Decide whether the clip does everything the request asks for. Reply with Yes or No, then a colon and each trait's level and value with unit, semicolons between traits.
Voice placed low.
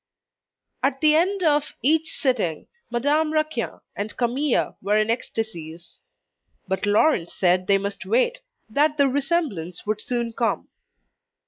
No: high, 245 Hz